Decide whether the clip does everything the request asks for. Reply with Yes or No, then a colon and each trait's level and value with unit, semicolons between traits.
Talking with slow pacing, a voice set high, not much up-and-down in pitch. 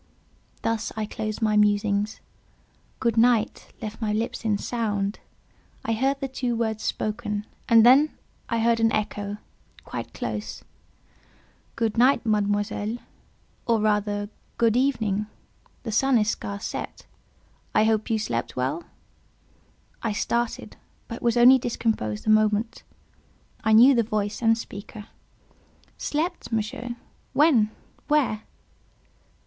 Yes: slow, 120 wpm; high, 220 Hz; narrow, 2.2 semitones